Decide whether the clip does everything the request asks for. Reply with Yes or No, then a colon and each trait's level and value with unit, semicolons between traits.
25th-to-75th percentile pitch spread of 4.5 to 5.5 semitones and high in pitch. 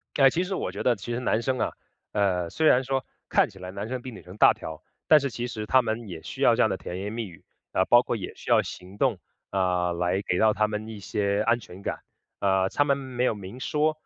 No: average, 5.0 semitones; low, 110 Hz